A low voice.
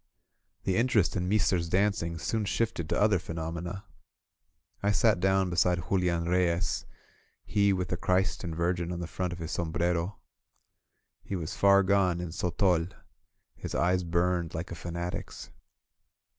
Yes: very low, 90 Hz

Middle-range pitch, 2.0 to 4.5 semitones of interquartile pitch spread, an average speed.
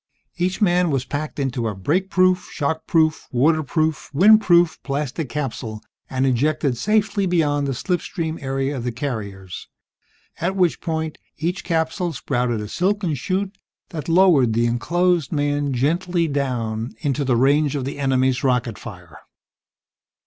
No: medium, 145 Hz; average, 5.2 semitones; average, 145 wpm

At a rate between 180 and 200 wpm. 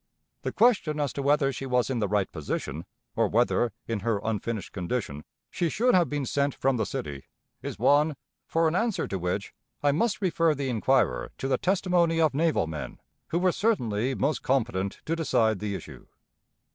Yes: average, 185 wpm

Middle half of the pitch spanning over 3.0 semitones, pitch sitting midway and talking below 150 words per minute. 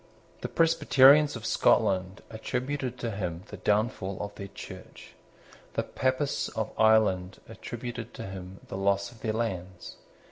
No: average, 3.9 semitones; low, 110 Hz; average, 140 wpm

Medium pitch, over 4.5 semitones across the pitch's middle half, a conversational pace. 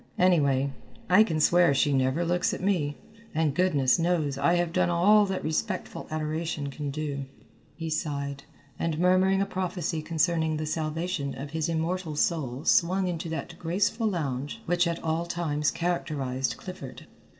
No: medium, 160 Hz; average, 3.3 semitones; average, 155 wpm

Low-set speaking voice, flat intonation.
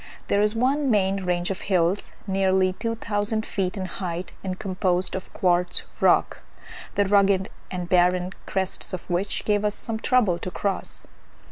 No: high, 190 Hz; narrow, 2.2 semitones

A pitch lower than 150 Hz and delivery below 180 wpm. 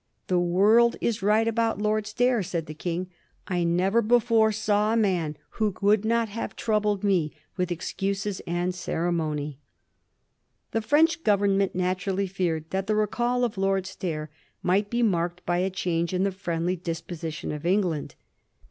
No: high, 195 Hz; average, 165 wpm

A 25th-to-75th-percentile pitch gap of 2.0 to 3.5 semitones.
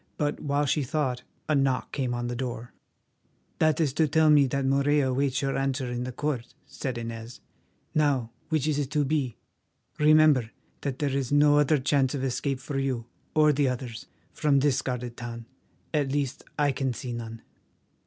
Yes: average, 2.8 semitones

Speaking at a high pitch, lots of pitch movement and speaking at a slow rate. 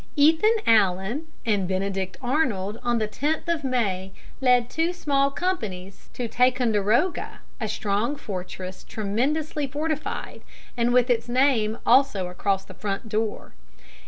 Yes: high, 235 Hz; wide, 5.8 semitones; slow, 130 wpm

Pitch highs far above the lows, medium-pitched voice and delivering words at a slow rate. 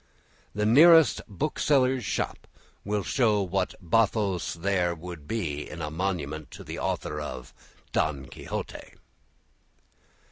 No: wide, 6.3 semitones; very low, 95 Hz; slow, 115 wpm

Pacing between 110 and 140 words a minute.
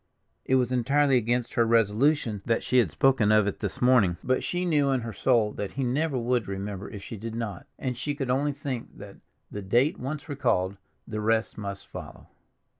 No: average, 200 wpm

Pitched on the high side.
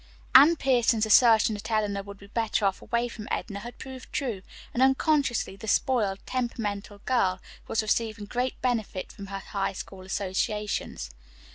Yes: high, 220 Hz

